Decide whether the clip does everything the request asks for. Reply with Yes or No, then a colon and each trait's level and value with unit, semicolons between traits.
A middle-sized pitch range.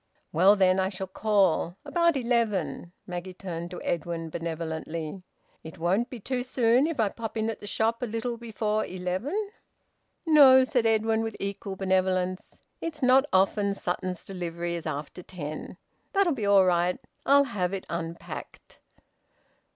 Yes: average, 4.8 semitones